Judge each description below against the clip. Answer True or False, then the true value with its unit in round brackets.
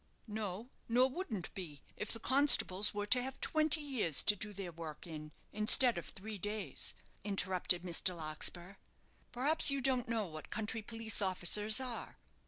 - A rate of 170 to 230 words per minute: False (160 wpm)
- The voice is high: True (210 Hz)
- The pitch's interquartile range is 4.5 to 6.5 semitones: True (5.2 semitones)